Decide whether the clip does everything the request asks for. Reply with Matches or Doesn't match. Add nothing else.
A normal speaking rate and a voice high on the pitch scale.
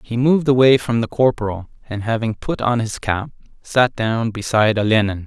Doesn't match